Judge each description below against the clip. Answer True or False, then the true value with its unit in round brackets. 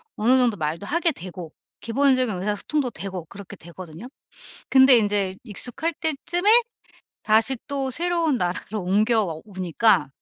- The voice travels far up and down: True (6.3 semitones)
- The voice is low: False (215 Hz)